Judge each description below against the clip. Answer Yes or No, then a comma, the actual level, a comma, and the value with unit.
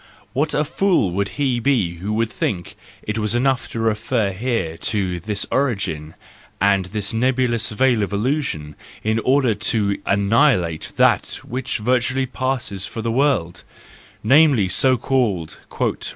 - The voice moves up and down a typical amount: Yes, average, 4.7 semitones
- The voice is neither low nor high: No, low, 110 Hz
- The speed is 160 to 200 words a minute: No, slow, 135 wpm